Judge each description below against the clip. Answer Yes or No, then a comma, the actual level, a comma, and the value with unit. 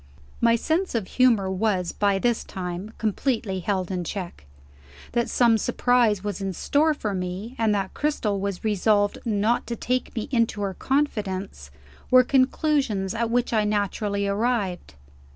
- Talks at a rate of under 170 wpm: Yes, average, 150 wpm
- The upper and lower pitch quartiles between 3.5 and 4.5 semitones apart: Yes, average, 3.8 semitones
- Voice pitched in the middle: No, high, 210 Hz